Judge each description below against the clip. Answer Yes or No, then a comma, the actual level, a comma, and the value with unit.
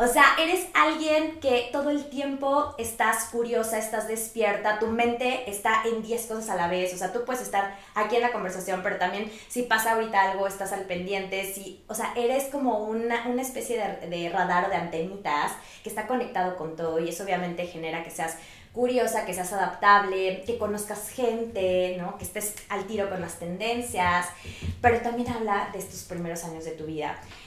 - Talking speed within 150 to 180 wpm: No, fast, 190 wpm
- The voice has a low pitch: No, high, 210 Hz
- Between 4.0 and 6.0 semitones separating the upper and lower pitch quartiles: Yes, average, 4.4 semitones